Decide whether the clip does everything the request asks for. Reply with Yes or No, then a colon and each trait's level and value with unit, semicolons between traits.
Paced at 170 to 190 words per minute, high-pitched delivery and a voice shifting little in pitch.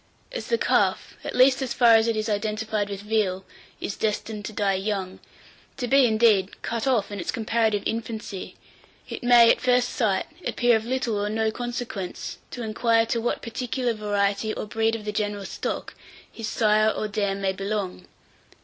Yes: average, 180 wpm; high, 220 Hz; narrow, 2.3 semitones